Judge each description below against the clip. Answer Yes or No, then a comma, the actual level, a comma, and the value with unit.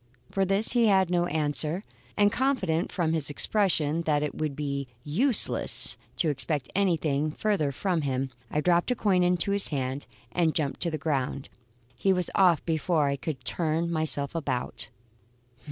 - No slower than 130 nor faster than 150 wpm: No, average, 165 wpm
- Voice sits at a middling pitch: Yes, medium, 160 Hz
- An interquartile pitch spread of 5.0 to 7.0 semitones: No, average, 4.1 semitones